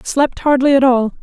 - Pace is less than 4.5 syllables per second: No, 4.7 syllables/s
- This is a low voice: No, very high, 265 Hz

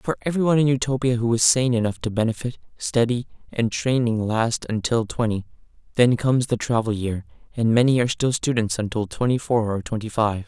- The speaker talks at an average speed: Yes, average, 185 wpm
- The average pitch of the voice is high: No, low, 115 Hz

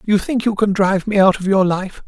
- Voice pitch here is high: Yes, high, 195 Hz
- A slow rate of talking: No, fast, 290 wpm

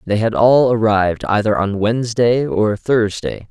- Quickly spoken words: No, average, 155 wpm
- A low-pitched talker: Yes, low, 110 Hz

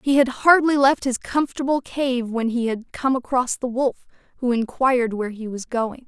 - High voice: Yes, very high, 250 Hz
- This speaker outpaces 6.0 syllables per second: No, 5.0 syllables/s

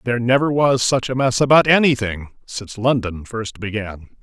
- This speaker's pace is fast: No, average, 170 wpm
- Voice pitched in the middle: No, low, 120 Hz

